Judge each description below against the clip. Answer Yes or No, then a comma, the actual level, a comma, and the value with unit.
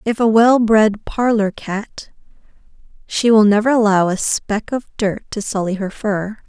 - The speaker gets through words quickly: No, average, 165 wpm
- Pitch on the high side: Yes, high, 215 Hz